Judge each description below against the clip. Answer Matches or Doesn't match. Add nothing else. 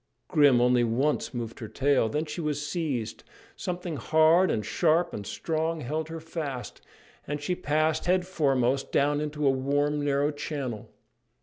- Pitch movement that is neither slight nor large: Matches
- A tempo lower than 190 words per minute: Matches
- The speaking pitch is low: Doesn't match